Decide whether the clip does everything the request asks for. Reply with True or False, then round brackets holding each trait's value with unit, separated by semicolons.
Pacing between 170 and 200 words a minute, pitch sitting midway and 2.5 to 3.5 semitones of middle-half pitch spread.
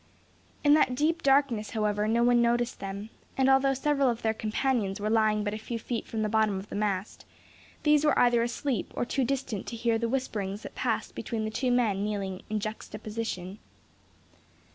False (190 wpm; 225 Hz; 3.2 semitones)